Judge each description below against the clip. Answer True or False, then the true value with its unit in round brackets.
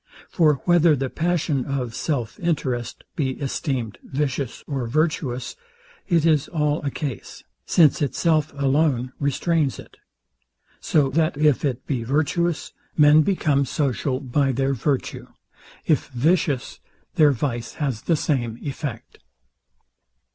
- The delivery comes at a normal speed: False (125 wpm)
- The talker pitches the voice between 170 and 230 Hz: False (140 Hz)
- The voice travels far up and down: False (3.1 semitones)